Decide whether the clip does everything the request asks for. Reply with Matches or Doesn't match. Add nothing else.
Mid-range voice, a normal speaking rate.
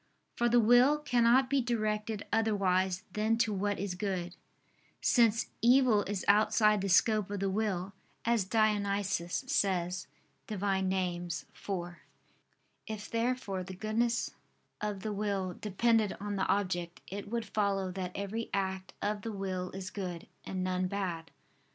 Doesn't match